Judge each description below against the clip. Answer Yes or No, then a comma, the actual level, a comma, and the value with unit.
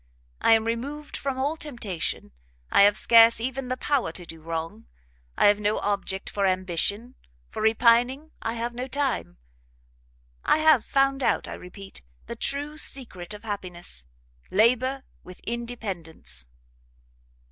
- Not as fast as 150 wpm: Yes, average, 140 wpm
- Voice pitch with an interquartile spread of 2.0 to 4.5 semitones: No, wide, 5.6 semitones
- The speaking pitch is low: No, high, 225 Hz